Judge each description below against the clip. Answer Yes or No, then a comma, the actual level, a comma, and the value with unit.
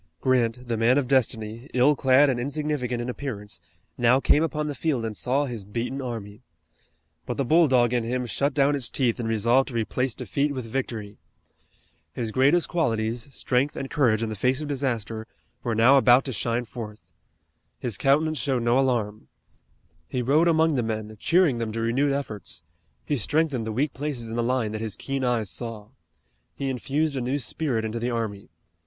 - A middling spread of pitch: Yes, average, 3.4 semitones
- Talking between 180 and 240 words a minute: Yes, average, 185 wpm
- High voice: No, low, 125 Hz